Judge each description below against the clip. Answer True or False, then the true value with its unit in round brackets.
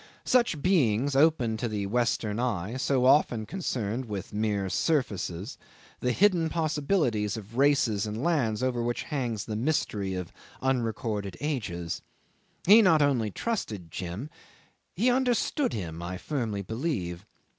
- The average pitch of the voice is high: False (120 Hz)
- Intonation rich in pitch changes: True (6.3 semitones)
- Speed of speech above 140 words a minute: False (135 wpm)